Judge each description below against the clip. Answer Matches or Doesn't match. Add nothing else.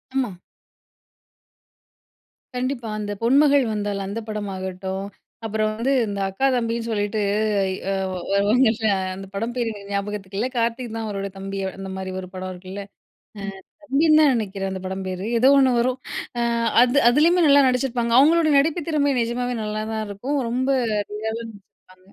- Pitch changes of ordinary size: Matches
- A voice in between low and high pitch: Doesn't match